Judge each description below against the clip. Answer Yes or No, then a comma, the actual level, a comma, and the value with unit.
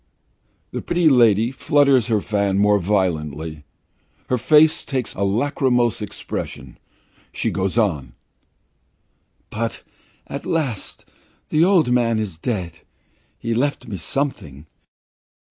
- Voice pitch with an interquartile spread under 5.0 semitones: No, wide, 5.6 semitones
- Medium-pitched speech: No, low, 115 Hz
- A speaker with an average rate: No, slow, 110 wpm